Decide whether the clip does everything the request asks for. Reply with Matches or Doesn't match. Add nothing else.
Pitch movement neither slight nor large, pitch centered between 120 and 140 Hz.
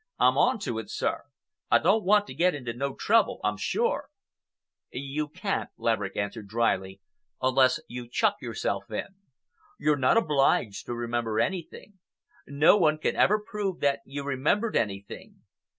Doesn't match